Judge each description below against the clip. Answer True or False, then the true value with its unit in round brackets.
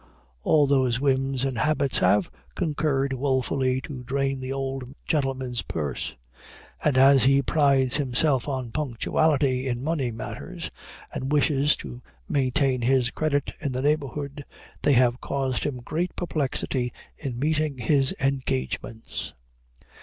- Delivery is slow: True (130 wpm)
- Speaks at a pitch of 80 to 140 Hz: True (135 Hz)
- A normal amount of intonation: False (2.1 semitones)